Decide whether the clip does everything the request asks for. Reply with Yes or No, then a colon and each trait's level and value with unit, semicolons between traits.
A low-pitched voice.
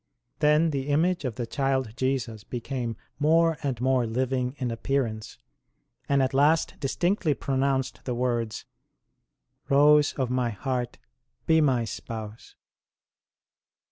Yes: low, 130 Hz